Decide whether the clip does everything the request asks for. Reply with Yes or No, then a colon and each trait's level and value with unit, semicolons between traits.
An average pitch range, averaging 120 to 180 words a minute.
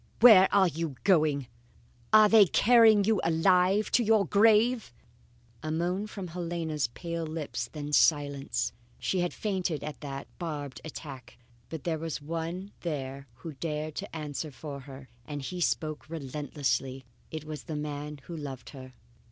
Yes: average, 4.1 semitones; average, 150 wpm